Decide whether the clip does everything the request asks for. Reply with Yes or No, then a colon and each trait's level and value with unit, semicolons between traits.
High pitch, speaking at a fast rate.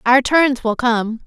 No: high, 245 Hz; average, 190 wpm